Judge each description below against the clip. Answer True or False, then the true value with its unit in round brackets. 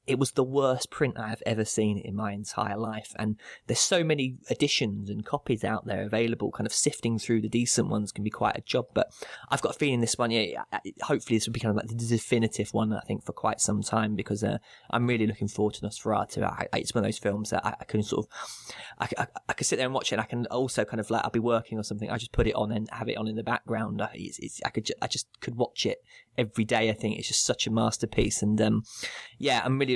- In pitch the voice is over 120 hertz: False (110 Hz)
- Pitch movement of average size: False (2.3 semitones)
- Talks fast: True (265 wpm)